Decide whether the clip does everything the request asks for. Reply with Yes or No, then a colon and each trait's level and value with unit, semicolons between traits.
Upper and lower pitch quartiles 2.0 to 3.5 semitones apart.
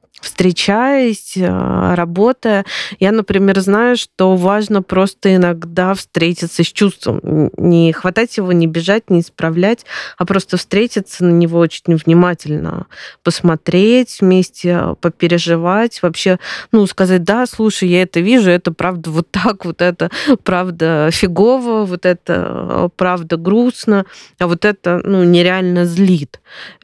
Yes: average, 2.9 semitones